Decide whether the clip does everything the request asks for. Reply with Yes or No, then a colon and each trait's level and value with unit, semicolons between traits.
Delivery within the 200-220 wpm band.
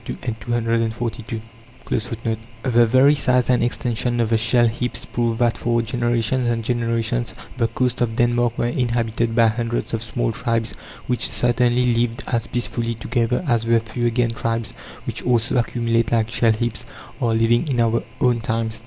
No: average, 155 wpm